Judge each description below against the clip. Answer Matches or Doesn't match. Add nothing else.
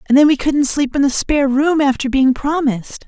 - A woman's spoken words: Matches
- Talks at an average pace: Doesn't match